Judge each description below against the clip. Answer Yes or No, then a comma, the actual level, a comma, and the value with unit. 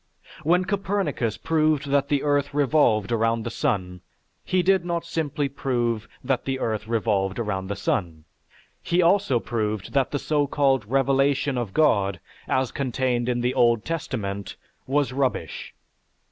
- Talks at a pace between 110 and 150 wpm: Yes, average, 145 wpm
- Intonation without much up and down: No, average, 4.8 semitones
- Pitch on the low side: Yes, low, 130 Hz